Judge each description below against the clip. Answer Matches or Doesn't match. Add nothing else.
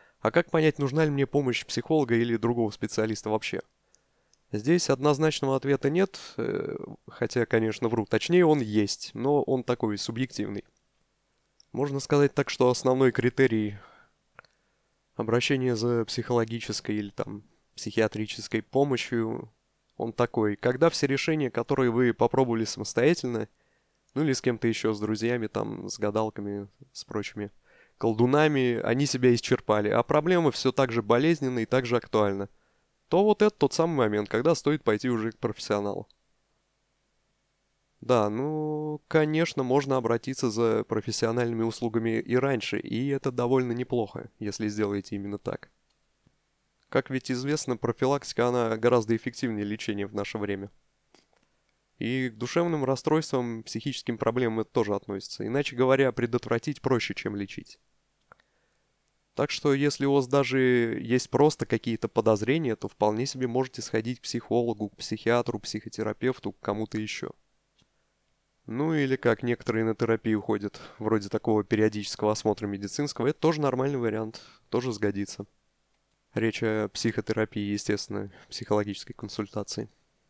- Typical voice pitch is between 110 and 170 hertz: Matches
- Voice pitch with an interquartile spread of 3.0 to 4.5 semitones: Matches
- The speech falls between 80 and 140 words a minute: Matches